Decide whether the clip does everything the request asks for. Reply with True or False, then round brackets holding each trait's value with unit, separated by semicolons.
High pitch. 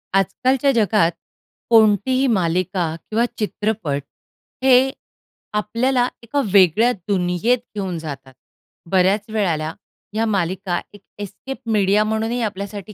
True (205 Hz)